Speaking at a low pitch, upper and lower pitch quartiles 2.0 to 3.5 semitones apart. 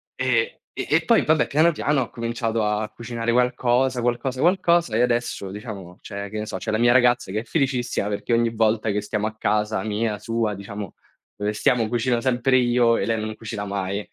Yes: low, 115 Hz; narrow, 2.6 semitones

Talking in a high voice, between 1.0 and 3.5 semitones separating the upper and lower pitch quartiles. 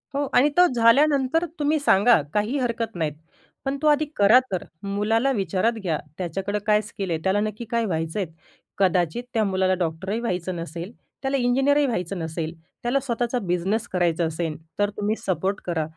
No: high, 205 Hz; wide, 5.4 semitones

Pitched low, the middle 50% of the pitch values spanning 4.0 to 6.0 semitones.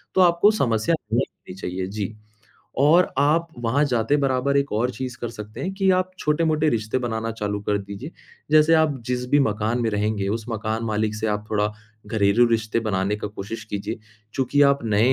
Yes: low, 115 Hz; average, 4.9 semitones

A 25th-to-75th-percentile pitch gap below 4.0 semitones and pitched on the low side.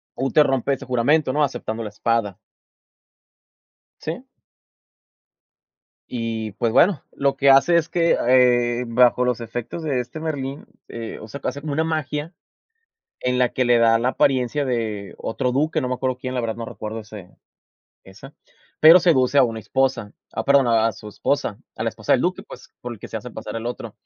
Yes: average, 3.5 semitones; low, 125 Hz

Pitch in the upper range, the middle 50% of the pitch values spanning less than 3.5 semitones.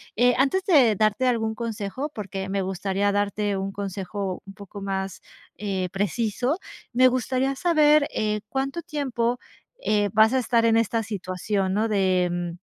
No: high, 210 Hz; average, 4.1 semitones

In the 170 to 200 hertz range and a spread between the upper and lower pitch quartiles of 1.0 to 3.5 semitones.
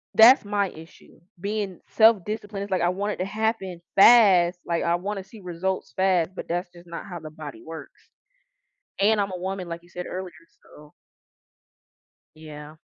Yes: medium, 185 Hz; average, 2.9 semitones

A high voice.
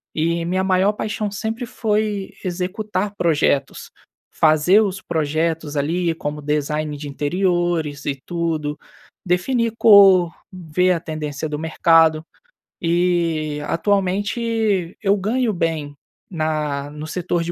No: medium, 170 Hz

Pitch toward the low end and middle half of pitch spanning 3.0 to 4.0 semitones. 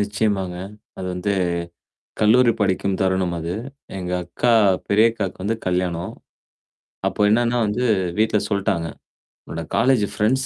Yes: low, 100 Hz; average, 3.3 semitones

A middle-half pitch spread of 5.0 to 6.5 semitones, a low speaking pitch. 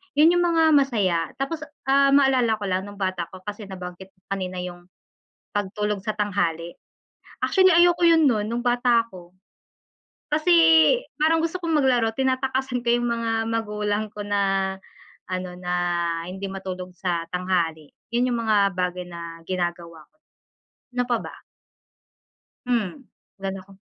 No: wide, 5.5 semitones; high, 205 Hz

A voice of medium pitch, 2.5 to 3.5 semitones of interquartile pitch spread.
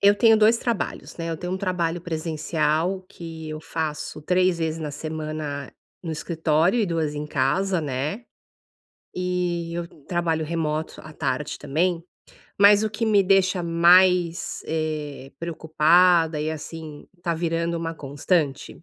Yes: medium, 165 Hz; average, 2.8 semitones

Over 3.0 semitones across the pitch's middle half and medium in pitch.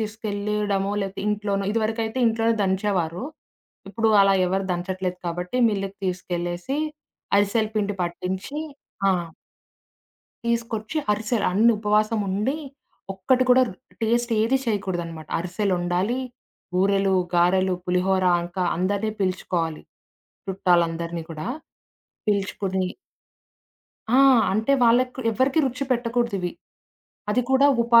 No: average, 3.6 semitones; high, 200 Hz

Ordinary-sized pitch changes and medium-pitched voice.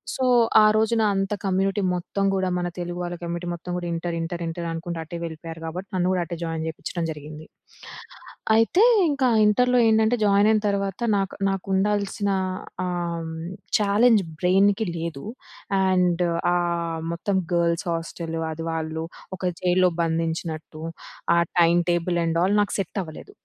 Yes: average, 3.0 semitones; medium, 175 Hz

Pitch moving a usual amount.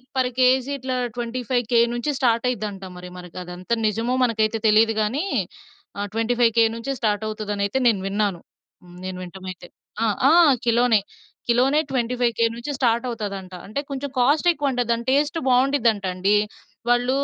Yes: average, 3.2 semitones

